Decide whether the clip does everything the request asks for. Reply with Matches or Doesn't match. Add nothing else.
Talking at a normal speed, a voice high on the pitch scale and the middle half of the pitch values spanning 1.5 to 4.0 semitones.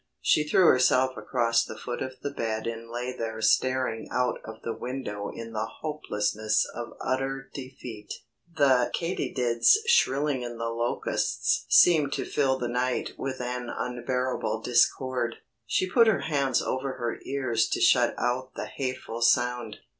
Doesn't match